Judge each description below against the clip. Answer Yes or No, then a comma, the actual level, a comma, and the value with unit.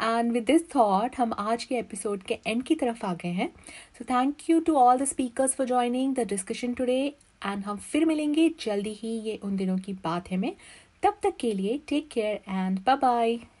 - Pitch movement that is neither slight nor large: Yes, average, 4.2 semitones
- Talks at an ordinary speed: No, fast, 215 wpm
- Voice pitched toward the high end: Yes, high, 240 Hz